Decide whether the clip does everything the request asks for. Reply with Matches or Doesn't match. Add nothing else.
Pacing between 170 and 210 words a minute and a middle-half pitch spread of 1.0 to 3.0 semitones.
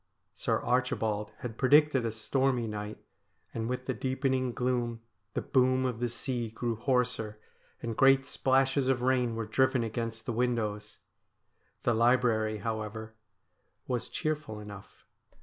Doesn't match